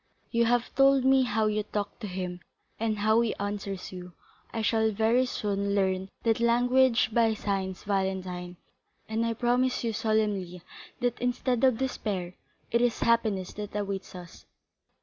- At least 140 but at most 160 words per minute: Yes, average, 155 wpm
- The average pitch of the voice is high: Yes, high, 215 Hz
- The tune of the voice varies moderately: Yes, average, 3.2 semitones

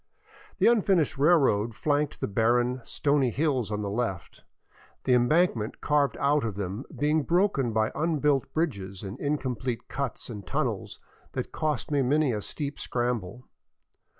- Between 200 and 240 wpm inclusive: No, average, 145 wpm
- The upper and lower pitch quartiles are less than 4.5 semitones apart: No, average, 5.0 semitones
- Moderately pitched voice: No, low, 130 Hz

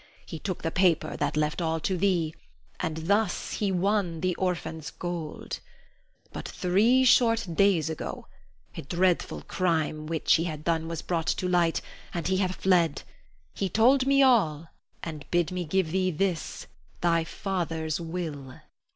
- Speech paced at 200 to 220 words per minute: No, average, 155 wpm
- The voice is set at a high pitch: No, medium, 175 Hz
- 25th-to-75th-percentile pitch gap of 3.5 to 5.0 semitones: No, average, 2.9 semitones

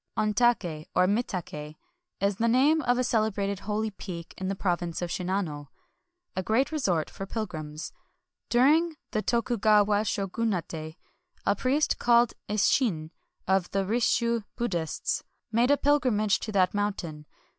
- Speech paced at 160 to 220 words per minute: No, average, 140 wpm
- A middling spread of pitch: Yes, average, 4.6 semitones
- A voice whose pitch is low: No, high, 205 Hz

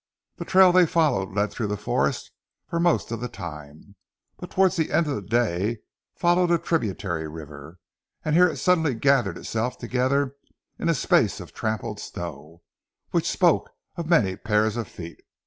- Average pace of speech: Yes, average, 170 wpm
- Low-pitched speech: Yes, low, 115 Hz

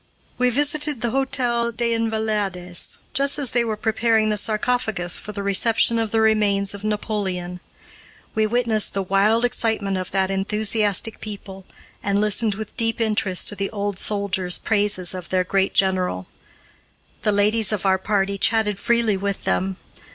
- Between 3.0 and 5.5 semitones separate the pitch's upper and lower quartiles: No, narrow, 2.6 semitones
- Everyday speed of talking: Yes, average, 160 wpm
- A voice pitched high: Yes, high, 210 Hz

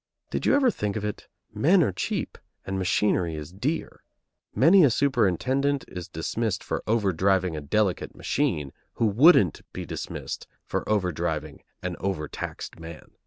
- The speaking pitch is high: No, low, 100 Hz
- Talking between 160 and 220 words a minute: No, average, 145 wpm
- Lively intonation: Yes, wide, 6.6 semitones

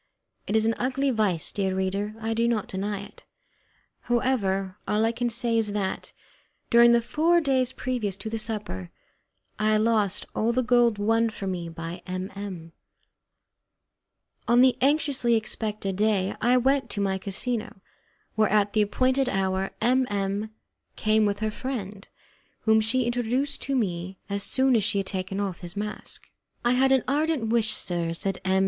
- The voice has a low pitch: No, high, 215 Hz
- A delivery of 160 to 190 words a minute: Yes, average, 170 wpm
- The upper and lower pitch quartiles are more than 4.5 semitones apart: No, average, 3.7 semitones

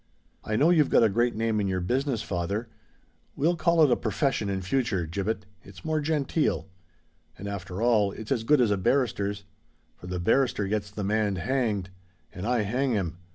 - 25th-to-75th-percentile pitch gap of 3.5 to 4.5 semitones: No, average, 4.9 semitones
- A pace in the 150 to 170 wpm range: No, average, 180 wpm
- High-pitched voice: No, low, 105 Hz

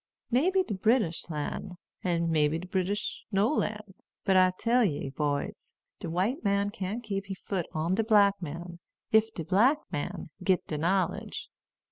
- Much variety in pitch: No, average, 4.1 semitones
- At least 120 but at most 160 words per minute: No, average, 175 wpm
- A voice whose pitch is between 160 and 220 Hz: Yes, high, 190 Hz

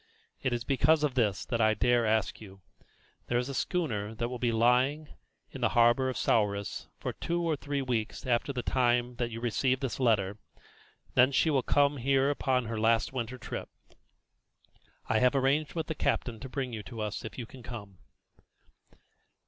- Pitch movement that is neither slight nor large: Yes, average, 3.1 semitones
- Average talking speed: Yes, average, 190 wpm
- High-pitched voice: No, low, 125 Hz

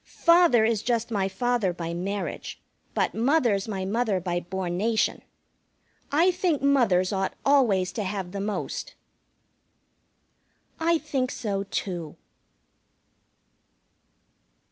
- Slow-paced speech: Yes, slow, 105 wpm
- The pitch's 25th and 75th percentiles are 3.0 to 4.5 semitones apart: No, average, 5.0 semitones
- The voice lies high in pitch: Yes, high, 210 Hz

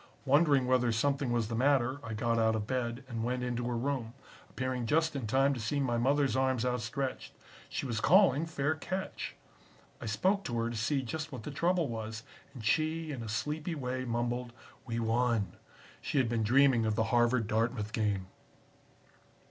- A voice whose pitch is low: Yes, low, 125 Hz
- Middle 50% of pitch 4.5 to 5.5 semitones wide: No, average, 3.5 semitones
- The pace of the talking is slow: No, average, 185 wpm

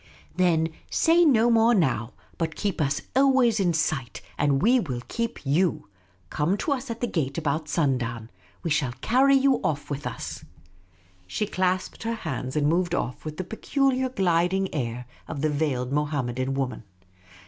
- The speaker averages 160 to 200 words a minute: Yes, average, 170 wpm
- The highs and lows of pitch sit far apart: Yes, wide, 8.1 semitones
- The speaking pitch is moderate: Yes, medium, 165 Hz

